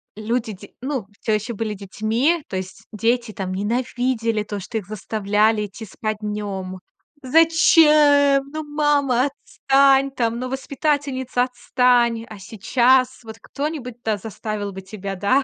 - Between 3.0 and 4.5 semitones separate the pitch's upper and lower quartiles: Yes, average, 4.2 semitones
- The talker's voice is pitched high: Yes, high, 235 Hz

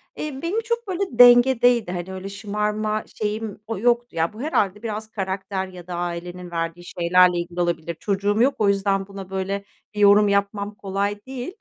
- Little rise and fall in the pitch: No, average, 3.4 semitones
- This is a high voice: Yes, high, 200 Hz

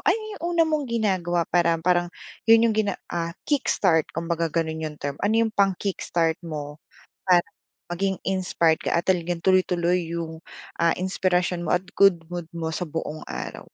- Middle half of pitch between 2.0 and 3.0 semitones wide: Yes, narrow, 2.5 semitones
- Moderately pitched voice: Yes, medium, 175 Hz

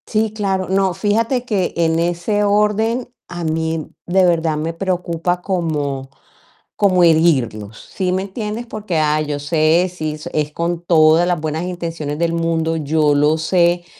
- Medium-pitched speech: Yes, medium, 170 Hz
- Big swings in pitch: No, average, 3.2 semitones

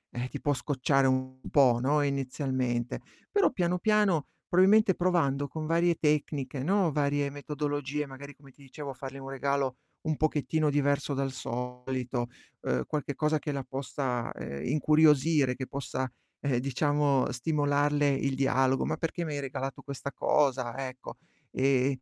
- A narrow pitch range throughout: Yes, narrow, 2.2 semitones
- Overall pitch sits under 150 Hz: Yes, medium, 140 Hz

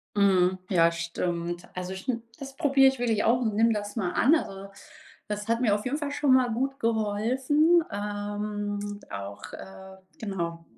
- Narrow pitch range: No, average, 4.6 semitones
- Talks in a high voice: Yes, high, 205 Hz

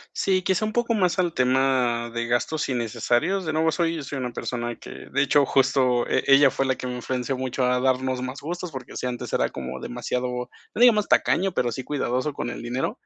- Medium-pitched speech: No, low, 130 Hz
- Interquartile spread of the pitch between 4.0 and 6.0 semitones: Yes, average, 4.4 semitones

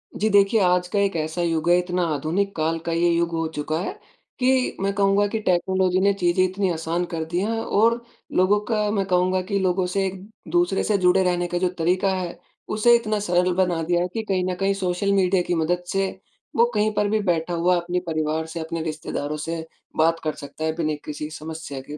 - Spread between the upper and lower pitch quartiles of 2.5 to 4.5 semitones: Yes, average, 3.0 semitones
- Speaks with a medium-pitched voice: Yes, medium, 180 Hz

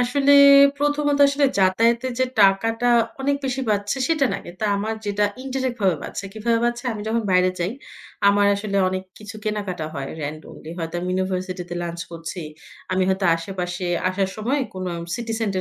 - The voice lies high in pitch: Yes, high, 200 Hz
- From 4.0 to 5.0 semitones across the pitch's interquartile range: Yes, average, 4.3 semitones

